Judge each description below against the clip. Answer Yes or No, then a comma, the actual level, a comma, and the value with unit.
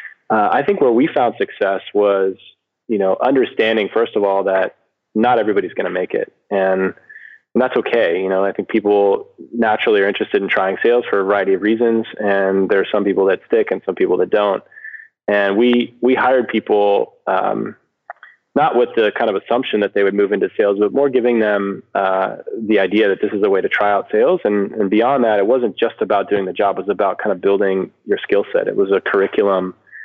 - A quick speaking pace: Yes, fast, 220 wpm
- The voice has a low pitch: Yes, low, 105 Hz